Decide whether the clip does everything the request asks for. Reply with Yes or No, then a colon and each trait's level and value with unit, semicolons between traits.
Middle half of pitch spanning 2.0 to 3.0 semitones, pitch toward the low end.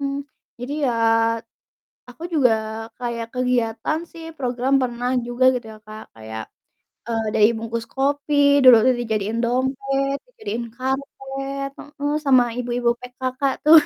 No: narrow, 2.6 semitones; very high, 255 Hz